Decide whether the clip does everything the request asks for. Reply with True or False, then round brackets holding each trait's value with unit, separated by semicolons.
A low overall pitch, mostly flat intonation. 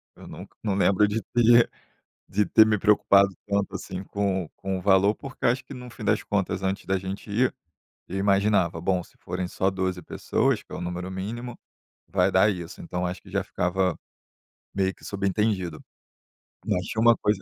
True (95 Hz; 2.2 semitones)